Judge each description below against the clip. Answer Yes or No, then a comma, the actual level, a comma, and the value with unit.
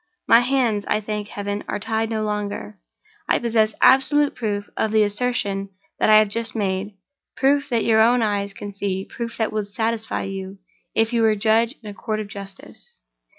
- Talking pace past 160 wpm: Yes, average, 180 wpm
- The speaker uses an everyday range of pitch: No, narrow, 2.2 semitones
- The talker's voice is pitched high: Yes, high, 215 Hz